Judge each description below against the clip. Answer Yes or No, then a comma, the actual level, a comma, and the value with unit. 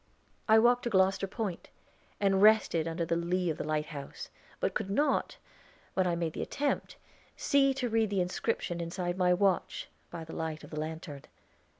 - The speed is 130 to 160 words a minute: No, average, 180 wpm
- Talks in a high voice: No, medium, 180 Hz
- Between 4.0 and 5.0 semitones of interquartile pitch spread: Yes, average, 4.4 semitones